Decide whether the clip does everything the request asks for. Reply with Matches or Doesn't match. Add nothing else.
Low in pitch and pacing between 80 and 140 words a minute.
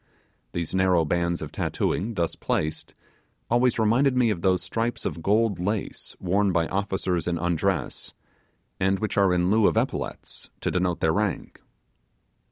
Doesn't match